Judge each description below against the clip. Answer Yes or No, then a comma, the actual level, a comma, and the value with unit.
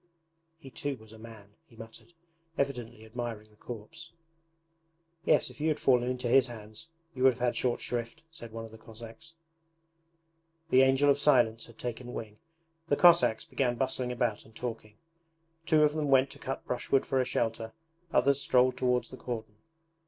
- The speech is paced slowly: No, average, 175 wpm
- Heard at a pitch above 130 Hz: No, low, 125 Hz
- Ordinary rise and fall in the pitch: Yes, average, 3.0 semitones